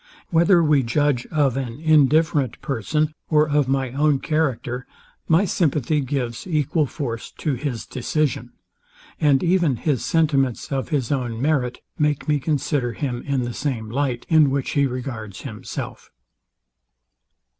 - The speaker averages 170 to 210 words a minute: No, average, 140 wpm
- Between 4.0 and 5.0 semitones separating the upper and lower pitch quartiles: No, average, 3.5 semitones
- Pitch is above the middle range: No, medium, 140 Hz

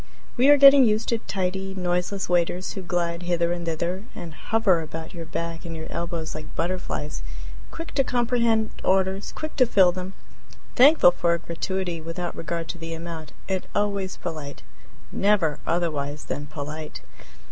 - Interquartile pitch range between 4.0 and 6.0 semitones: No, average, 3.0 semitones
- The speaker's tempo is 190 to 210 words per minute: No, average, 160 wpm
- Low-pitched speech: No, medium, 175 Hz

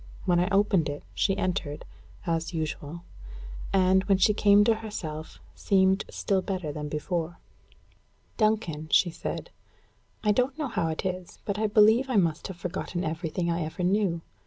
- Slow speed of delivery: No, average, 160 wpm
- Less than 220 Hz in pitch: Yes, medium, 185 Hz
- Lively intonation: No, average, 3.9 semitones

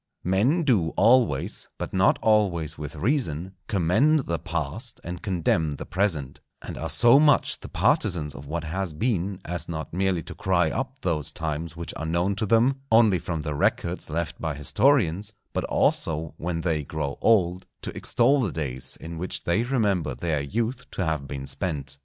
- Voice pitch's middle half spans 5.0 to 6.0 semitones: Yes, wide, 5.6 semitones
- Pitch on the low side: Yes, very low, 85 Hz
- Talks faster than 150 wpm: Yes, average, 175 wpm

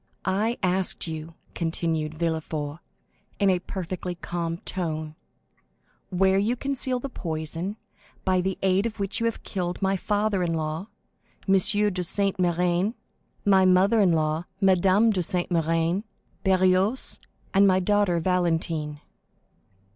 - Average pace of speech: No, slow, 130 wpm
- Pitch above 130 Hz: Yes, medium, 185 Hz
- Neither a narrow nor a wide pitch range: Yes, average, 3.0 semitones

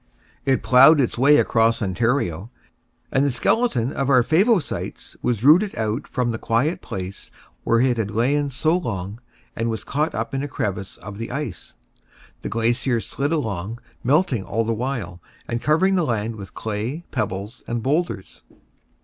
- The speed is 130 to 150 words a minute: No, average, 165 wpm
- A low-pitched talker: Yes, low, 120 Hz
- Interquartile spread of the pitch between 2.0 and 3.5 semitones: No, average, 4.4 semitones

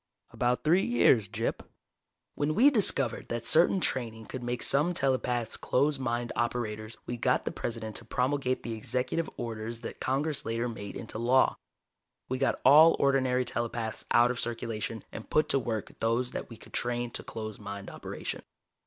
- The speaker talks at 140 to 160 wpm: No, average, 170 wpm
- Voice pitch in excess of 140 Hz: No, low, 120 Hz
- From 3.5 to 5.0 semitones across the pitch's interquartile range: No, average, 3.0 semitones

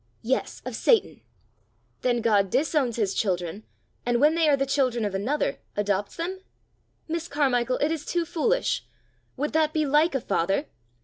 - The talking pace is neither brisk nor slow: Yes, average, 165 wpm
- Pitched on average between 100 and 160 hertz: No, very high, 270 Hz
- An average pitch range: No, wide, 6.1 semitones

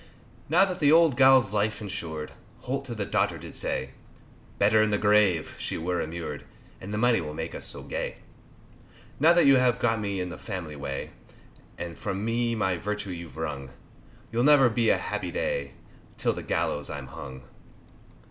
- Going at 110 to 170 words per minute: No, average, 185 wpm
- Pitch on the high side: No, low, 105 Hz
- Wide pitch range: Yes, wide, 6.7 semitones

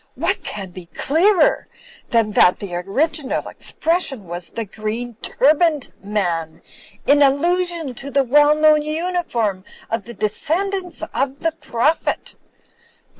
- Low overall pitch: No, very high, 275 Hz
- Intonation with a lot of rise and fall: Yes, wide, 7.2 semitones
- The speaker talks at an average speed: No, slow, 125 wpm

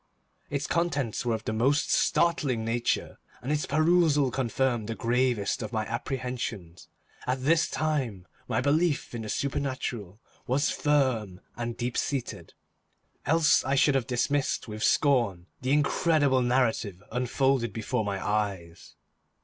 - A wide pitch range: No, average, 4.2 semitones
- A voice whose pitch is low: Yes, low, 125 Hz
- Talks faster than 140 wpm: No, slow, 135 wpm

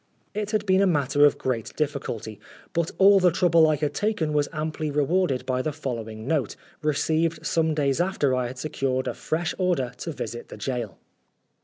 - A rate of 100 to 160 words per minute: No, average, 185 wpm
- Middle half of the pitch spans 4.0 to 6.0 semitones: Yes, average, 4.5 semitones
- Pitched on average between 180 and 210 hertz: No, medium, 150 Hz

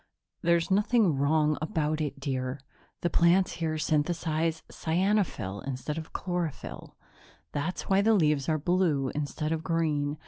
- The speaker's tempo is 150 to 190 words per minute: No, slow, 135 wpm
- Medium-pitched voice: Yes, medium, 160 Hz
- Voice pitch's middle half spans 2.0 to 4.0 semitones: Yes, average, 2.9 semitones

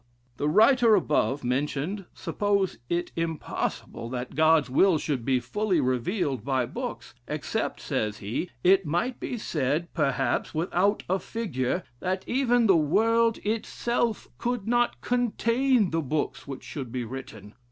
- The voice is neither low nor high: Yes, medium, 170 Hz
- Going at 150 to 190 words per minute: No, average, 140 wpm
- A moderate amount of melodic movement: No, wide, 8.2 semitones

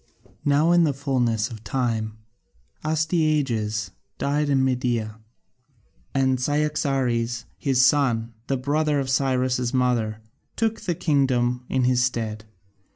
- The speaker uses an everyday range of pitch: Yes, average, 3.3 semitones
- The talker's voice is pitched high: No, low, 130 Hz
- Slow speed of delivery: Yes, slow, 115 wpm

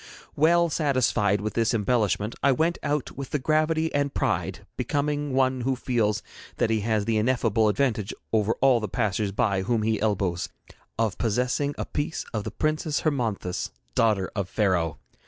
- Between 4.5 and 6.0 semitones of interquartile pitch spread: Yes, average, 5.1 semitones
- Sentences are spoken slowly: No, average, 165 wpm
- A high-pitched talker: No, low, 115 Hz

